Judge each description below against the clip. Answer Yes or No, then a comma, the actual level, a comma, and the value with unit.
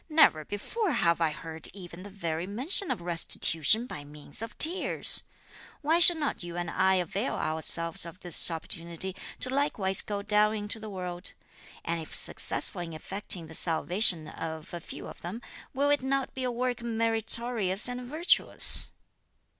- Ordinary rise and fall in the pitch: No, wide, 6.2 semitones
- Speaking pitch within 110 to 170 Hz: No, high, 195 Hz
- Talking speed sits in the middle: Yes, average, 165 wpm